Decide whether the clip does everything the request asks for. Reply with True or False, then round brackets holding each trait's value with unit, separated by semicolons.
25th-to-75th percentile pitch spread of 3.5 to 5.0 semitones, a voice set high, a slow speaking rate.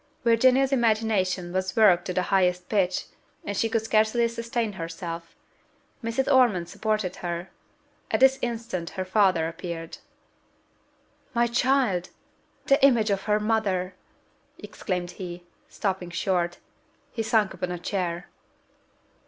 True (4.3 semitones; 195 Hz; 120 wpm)